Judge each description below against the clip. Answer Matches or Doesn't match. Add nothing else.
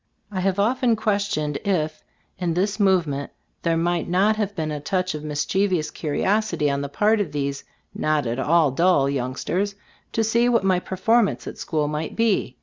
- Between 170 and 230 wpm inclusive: Matches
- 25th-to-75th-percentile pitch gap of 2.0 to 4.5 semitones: Doesn't match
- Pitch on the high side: Doesn't match